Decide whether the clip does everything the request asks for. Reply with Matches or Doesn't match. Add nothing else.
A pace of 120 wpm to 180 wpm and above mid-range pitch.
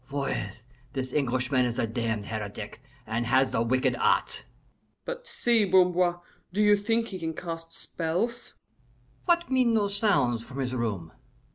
Doesn't match